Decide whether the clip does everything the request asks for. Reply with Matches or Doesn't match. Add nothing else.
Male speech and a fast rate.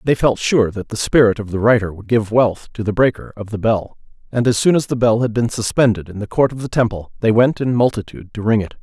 Matches